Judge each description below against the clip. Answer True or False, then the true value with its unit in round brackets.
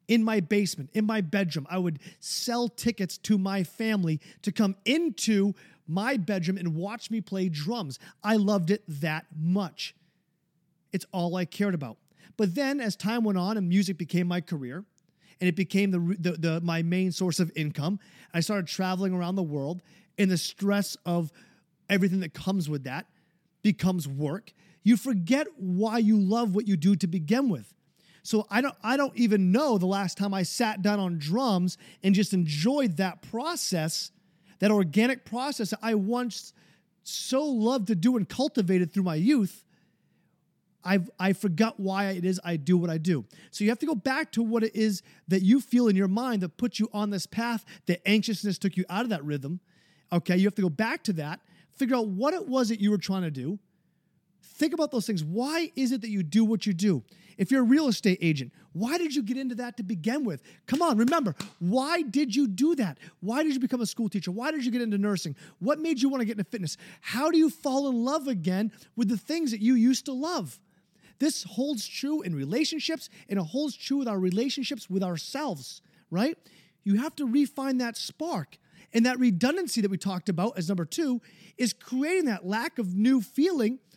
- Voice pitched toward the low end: False (200 Hz)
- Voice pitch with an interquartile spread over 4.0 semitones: True (4.8 semitones)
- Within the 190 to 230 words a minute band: True (205 wpm)